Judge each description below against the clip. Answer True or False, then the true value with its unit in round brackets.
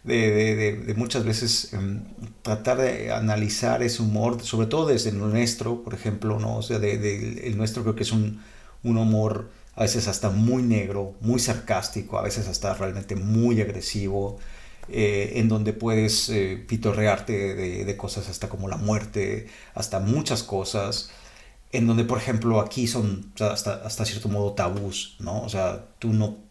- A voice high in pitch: False (110 Hz)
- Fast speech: False (180 wpm)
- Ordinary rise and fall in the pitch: False (2.0 semitones)